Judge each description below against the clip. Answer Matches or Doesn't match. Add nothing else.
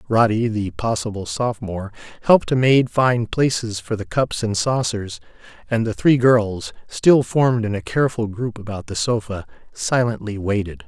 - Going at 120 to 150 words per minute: Doesn't match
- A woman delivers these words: Doesn't match